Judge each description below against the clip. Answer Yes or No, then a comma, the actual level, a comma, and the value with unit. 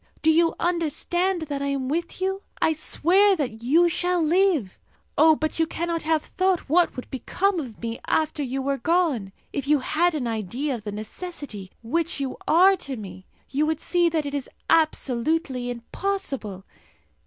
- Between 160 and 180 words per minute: Yes, average, 175 wpm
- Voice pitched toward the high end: Yes, very high, 305 Hz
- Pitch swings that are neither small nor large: Yes, average, 5.0 semitones